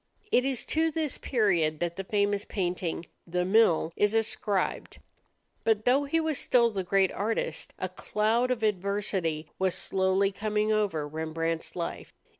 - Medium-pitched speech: No, high, 200 Hz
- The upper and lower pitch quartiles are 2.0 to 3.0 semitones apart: No, average, 4.2 semitones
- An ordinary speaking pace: Yes, average, 150 wpm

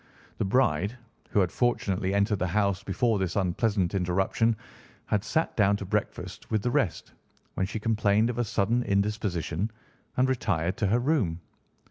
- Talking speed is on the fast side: No, average, 160 wpm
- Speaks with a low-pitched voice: Yes, low, 100 Hz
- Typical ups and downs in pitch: Yes, average, 3.2 semitones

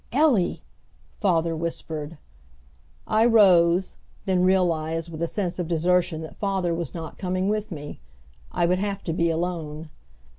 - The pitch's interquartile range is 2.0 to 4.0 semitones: Yes, narrow, 2.5 semitones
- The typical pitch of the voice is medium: Yes, medium, 175 Hz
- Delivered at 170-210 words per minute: No, average, 145 wpm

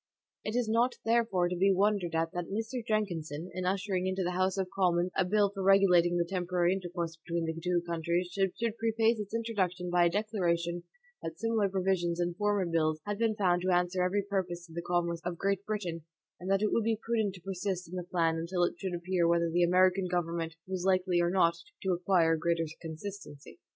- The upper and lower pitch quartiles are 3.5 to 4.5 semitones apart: No, narrow, 2.4 semitones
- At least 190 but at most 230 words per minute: Yes, fast, 205 wpm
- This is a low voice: No, medium, 180 Hz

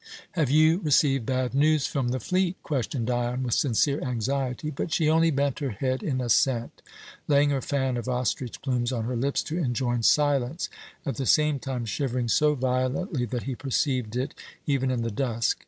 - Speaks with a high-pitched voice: No, low, 130 Hz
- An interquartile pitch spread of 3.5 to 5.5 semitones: No, average, 2.8 semitones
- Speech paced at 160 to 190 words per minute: Yes, average, 185 wpm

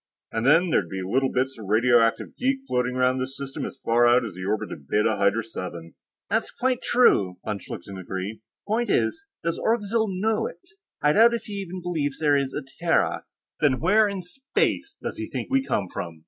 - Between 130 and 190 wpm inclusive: No, fast, 205 wpm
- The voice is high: No, low, 135 Hz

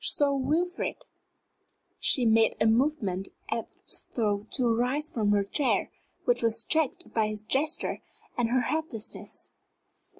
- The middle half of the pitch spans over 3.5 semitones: Yes, average, 4.9 semitones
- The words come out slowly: Yes, slow, 130 wpm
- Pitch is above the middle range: Yes, high, 240 Hz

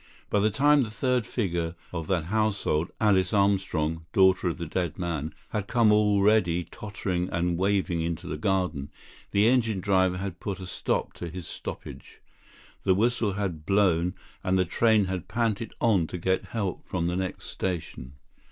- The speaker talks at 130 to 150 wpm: No, average, 170 wpm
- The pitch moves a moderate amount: Yes, average, 3.4 semitones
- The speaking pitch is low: Yes, very low, 95 Hz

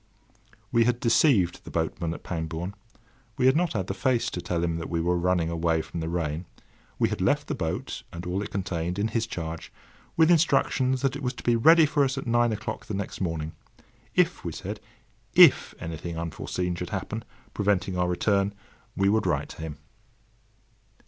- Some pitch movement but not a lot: No, wide, 5.8 semitones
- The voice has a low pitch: Yes, very low, 95 Hz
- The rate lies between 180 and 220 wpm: Yes, average, 190 wpm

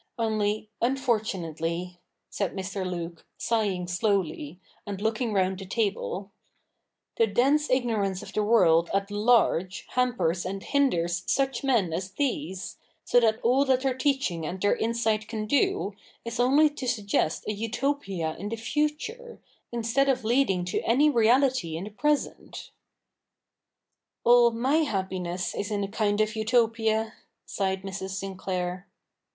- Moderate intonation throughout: Yes, average, 4.5 semitones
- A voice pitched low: No, high, 215 Hz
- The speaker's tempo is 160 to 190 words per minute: No, average, 145 wpm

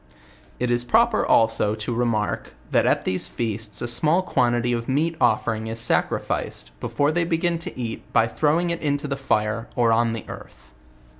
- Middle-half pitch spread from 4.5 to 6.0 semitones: Yes, average, 5.1 semitones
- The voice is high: No, low, 120 Hz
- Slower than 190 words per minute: Yes, average, 175 wpm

